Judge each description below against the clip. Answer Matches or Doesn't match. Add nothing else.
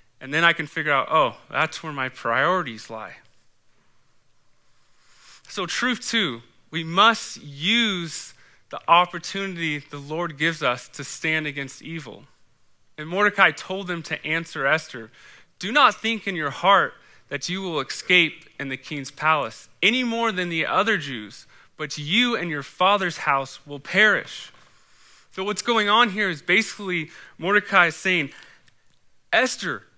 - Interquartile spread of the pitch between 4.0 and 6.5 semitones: Matches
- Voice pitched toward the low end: Doesn't match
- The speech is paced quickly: Doesn't match